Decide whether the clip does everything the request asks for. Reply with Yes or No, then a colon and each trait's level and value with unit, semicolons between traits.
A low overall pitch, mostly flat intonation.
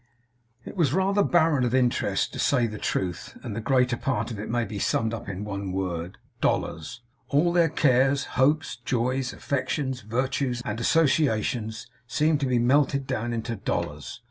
No: low, 125 Hz; average, 4.1 semitones